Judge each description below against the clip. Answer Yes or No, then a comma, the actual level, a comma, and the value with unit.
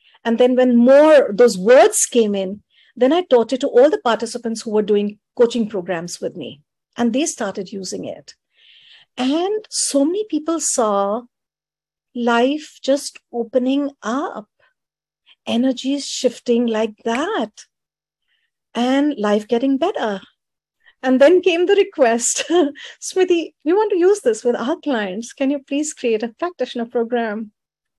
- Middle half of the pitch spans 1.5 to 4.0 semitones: No, average, 4.9 semitones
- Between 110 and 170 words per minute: Yes, average, 140 wpm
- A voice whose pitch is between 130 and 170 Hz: No, very high, 250 Hz